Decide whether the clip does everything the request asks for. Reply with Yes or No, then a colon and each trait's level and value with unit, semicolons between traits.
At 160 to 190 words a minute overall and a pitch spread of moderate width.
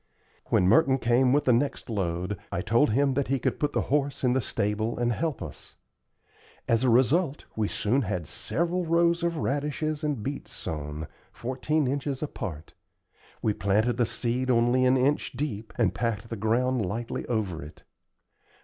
Yes: average, 170 wpm; average, 4.8 semitones